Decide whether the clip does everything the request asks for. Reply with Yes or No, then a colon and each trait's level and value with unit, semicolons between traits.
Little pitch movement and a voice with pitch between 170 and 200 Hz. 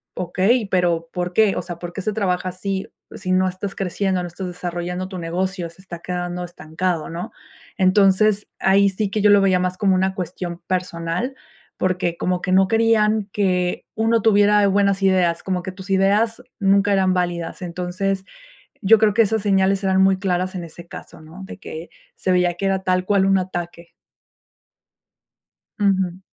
Yes: narrow, 1.9 semitones; medium, 185 Hz